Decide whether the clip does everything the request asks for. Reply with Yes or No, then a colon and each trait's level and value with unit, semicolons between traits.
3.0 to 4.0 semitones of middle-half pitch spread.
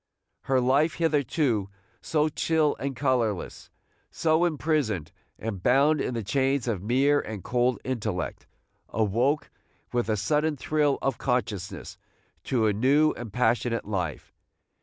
No: average, 5.0 semitones